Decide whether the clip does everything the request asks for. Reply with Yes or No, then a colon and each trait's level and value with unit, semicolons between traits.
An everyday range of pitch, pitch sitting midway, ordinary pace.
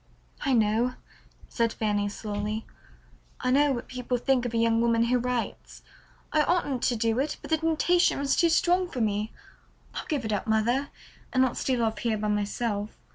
No: average, 3.7 semitones; high, 240 Hz; average, 185 wpm